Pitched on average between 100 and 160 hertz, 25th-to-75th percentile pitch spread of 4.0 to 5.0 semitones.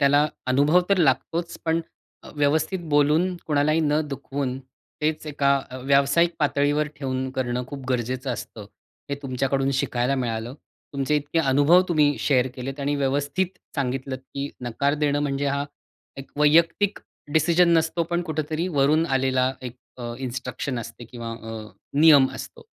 No: medium, 140 Hz; average, 2.8 semitones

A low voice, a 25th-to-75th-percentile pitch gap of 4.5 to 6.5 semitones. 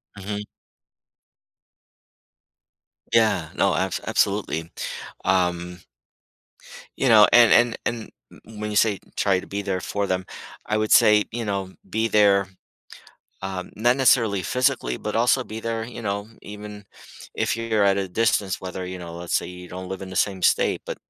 No: low, 100 Hz; average, 2.7 semitones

